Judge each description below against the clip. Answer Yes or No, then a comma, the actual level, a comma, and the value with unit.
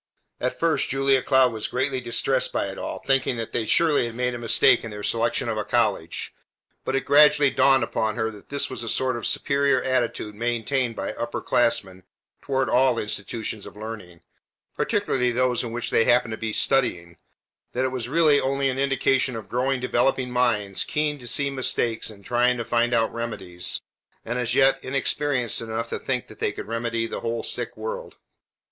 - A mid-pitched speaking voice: No, low, 120 Hz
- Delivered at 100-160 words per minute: No, average, 190 wpm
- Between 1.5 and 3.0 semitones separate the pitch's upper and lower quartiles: Yes, average, 2.7 semitones